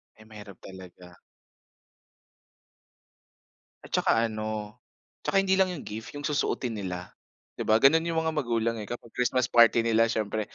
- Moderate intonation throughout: Yes, average, 3.7 semitones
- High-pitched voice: No, low, 115 Hz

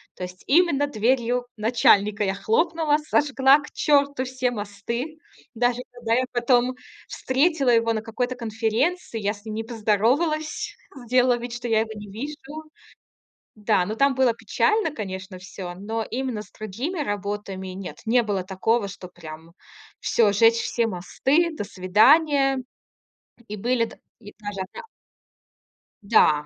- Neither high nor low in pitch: No, high, 230 Hz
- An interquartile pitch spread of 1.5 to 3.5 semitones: No, average, 4.6 semitones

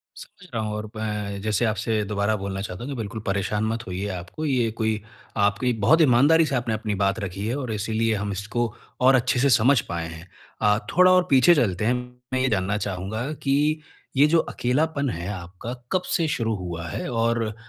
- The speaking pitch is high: No, low, 110 Hz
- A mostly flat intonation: No, average, 4.3 semitones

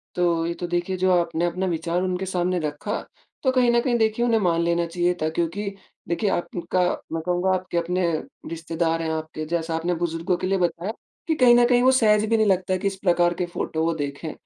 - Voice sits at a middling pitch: Yes, medium, 175 Hz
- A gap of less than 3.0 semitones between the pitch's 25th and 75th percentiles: Yes, narrow, 2.5 semitones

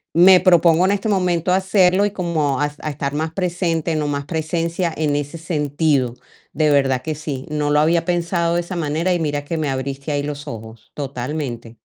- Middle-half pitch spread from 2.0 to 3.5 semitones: Yes, average, 3.2 semitones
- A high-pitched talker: No, medium, 155 Hz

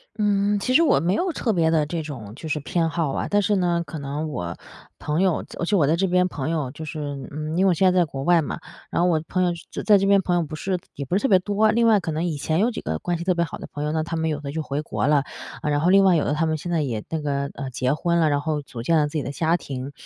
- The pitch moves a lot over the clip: No, average, 3.7 semitones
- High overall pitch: No, medium, 160 Hz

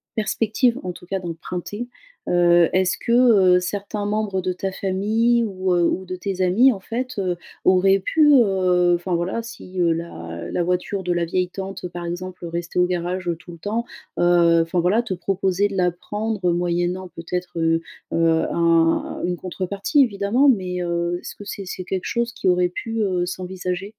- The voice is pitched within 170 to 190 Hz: Yes, medium, 185 Hz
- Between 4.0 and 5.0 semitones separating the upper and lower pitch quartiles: No, narrow, 2.4 semitones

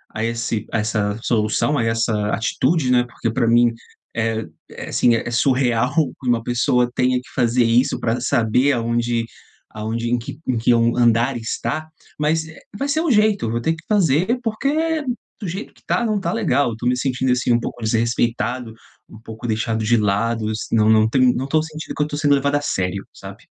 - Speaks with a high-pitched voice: No, low, 120 Hz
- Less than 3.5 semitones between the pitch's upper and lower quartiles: No, average, 3.9 semitones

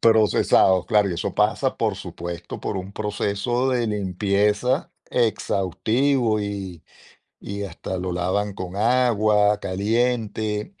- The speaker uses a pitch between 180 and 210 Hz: No, low, 105 Hz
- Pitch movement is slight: No, average, 3.0 semitones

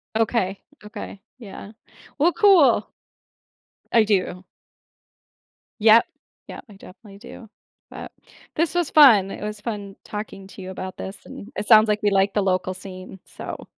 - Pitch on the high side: Yes, high, 210 Hz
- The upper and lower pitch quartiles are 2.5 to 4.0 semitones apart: Yes, average, 2.8 semitones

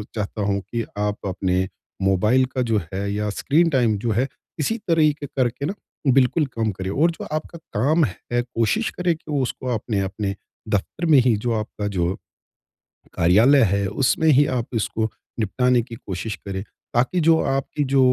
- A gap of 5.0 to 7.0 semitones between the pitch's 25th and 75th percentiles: Yes, wide, 5.5 semitones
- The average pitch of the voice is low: Yes, low, 120 Hz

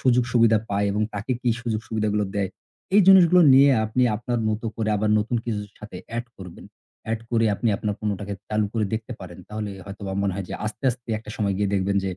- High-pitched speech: No, low, 110 Hz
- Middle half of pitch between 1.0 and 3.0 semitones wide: Yes, narrow, 2.5 semitones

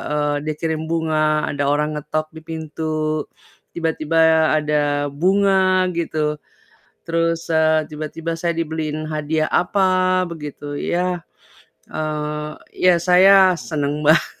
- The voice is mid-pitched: Yes, medium, 160 Hz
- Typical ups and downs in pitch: No, narrow, 1.8 semitones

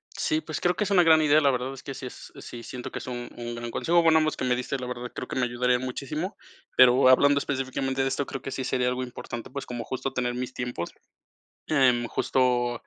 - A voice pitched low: Yes, low, 130 Hz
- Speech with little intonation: Yes, narrow, 2.3 semitones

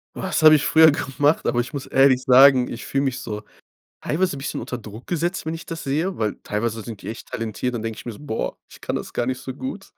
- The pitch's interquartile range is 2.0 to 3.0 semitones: No, average, 4.6 semitones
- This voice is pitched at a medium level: No, low, 130 Hz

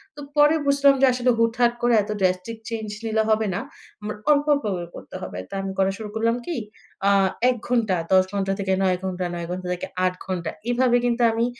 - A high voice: Yes, high, 220 Hz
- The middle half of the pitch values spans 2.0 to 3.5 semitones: No, average, 4.4 semitones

